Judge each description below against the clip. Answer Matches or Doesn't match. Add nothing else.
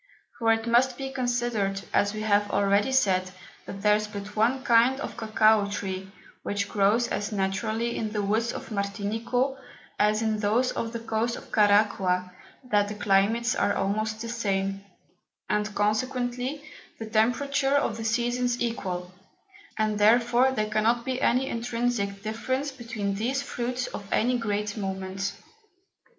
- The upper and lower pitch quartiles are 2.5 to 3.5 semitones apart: Matches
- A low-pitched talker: Doesn't match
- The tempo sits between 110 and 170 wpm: Matches